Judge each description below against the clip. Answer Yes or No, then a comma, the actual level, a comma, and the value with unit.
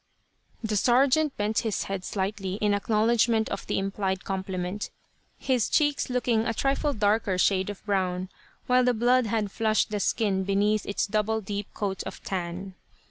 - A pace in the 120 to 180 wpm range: Yes, average, 160 wpm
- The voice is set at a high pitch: Yes, high, 210 Hz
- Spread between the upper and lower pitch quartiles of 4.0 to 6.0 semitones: No, average, 2.9 semitones